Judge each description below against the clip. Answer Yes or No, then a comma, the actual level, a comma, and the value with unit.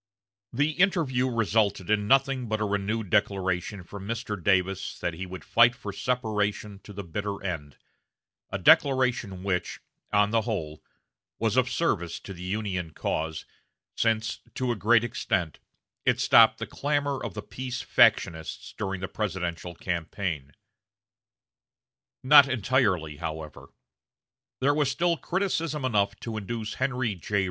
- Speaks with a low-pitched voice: Yes, low, 105 Hz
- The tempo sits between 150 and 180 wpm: No, average, 140 wpm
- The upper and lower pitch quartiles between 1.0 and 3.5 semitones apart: No, average, 5.1 semitones